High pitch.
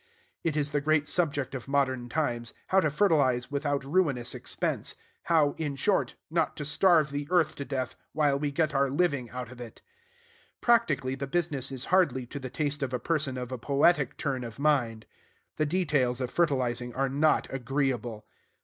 No: medium, 140 Hz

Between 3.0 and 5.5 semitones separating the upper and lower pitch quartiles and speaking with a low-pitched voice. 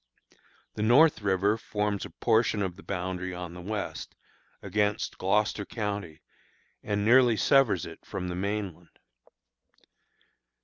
No: narrow, 2.6 semitones; low, 100 Hz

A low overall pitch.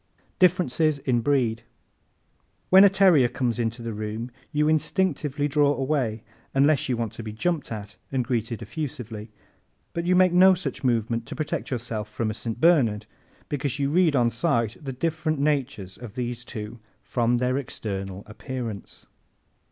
Yes: low, 125 Hz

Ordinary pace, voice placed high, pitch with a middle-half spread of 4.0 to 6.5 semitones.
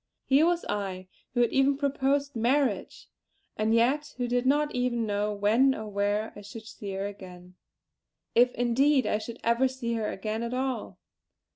Yes: average, 170 wpm; high, 235 Hz; average, 4.3 semitones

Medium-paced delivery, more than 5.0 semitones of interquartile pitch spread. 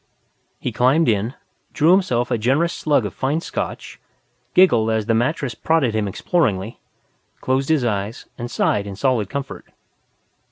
Yes: average, 150 wpm; wide, 5.4 semitones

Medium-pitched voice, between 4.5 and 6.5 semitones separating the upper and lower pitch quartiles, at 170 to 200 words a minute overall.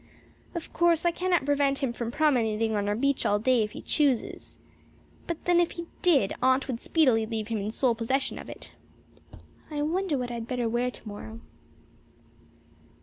No: very high, 255 Hz; average, 5.1 semitones; average, 180 wpm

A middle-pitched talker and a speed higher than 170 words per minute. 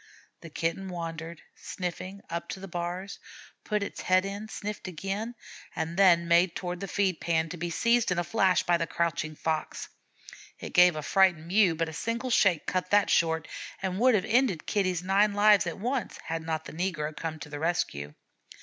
Yes: medium, 180 Hz; average, 190 wpm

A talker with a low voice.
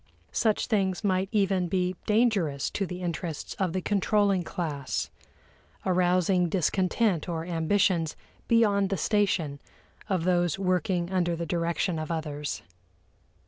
No: medium, 180 Hz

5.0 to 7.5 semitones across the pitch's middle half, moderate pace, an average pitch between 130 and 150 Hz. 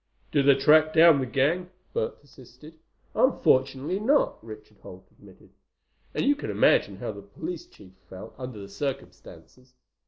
Yes: wide, 5.4 semitones; average, 150 wpm; medium, 140 Hz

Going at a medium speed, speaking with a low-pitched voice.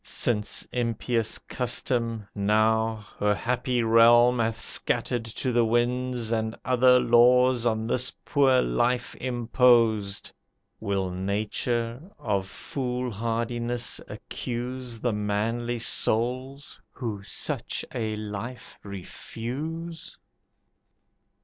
No: slow, 95 wpm; low, 120 Hz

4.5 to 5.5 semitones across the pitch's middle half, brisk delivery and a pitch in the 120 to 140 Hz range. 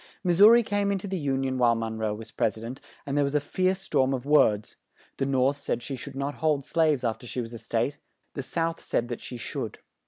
Yes: average, 4.9 semitones; fast, 255 wpm; low, 135 Hz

